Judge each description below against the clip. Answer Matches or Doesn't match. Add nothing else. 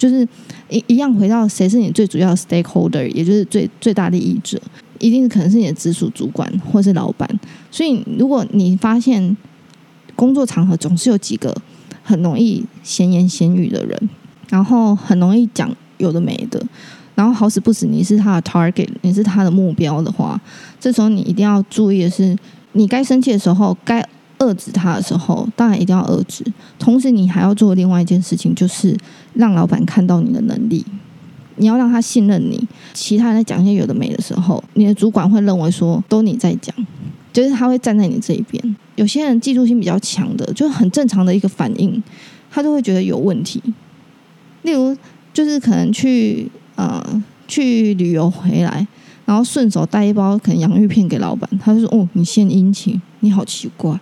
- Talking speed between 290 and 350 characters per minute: Matches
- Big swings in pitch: Doesn't match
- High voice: Matches